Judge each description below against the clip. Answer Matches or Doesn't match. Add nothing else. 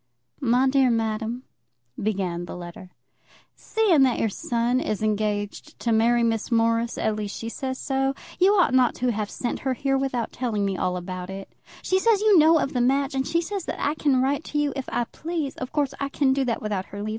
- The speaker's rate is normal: Doesn't match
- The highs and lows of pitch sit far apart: Doesn't match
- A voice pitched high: Matches